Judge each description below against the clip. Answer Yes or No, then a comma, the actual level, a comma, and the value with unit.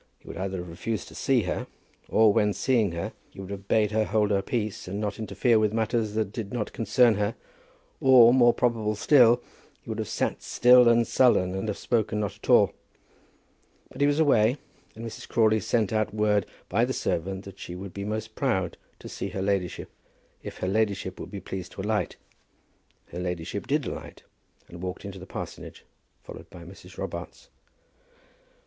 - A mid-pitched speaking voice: No, low, 105 Hz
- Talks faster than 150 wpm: Yes, average, 190 wpm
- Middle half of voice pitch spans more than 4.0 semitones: No, average, 3.0 semitones